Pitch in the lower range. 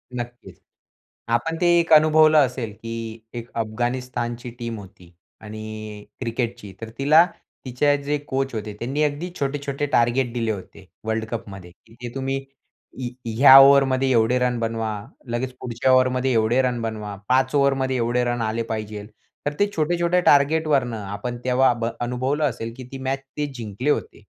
Yes: low, 125 Hz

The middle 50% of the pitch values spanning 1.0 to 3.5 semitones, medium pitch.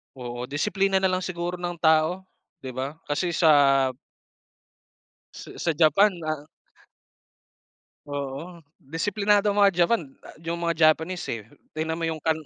No: average, 4.0 semitones; medium, 165 Hz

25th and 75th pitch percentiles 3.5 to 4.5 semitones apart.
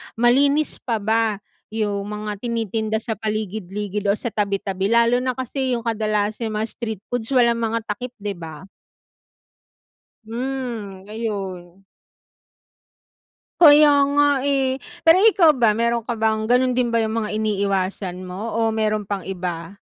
No: average, 3.0 semitones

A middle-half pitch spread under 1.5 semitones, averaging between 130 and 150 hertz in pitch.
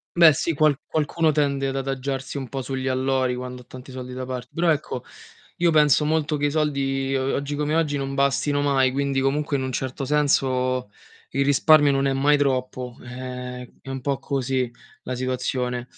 No: narrow, 2.1 semitones; low, 135 Hz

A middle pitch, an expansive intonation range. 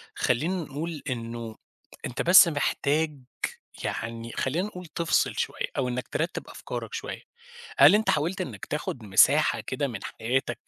Yes: medium, 145 Hz; wide, 6.2 semitones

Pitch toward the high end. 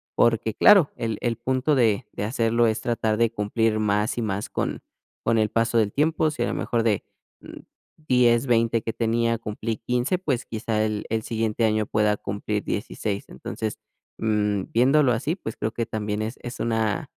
No: low, 115 Hz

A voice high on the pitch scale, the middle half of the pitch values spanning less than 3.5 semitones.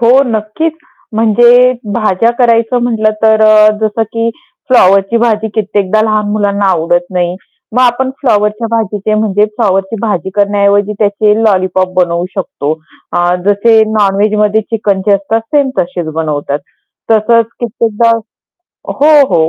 Yes: high, 215 Hz; average, 2.8 semitones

